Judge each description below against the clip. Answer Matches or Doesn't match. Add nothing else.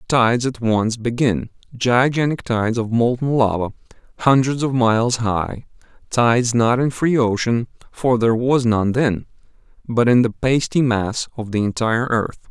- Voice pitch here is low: Matches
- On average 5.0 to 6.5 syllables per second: Doesn't match